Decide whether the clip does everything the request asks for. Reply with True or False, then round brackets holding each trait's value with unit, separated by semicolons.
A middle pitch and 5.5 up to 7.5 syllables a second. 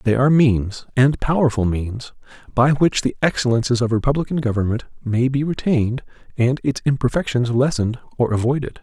False (125 Hz; 5.7 syllables/s)